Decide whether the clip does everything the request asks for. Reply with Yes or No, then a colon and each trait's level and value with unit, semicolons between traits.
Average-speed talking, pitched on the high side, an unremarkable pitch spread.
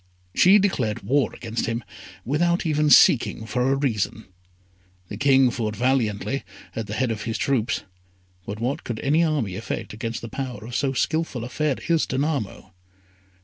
No: average, 165 wpm; low, 125 Hz; average, 4.3 semitones